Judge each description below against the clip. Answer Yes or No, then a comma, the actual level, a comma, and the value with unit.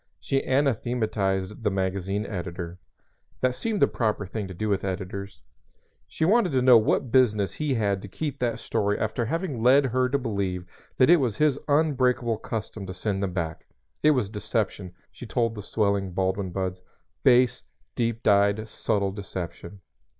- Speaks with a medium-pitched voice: No, low, 105 Hz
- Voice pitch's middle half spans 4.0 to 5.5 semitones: Yes, average, 4.6 semitones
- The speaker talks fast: No, average, 165 wpm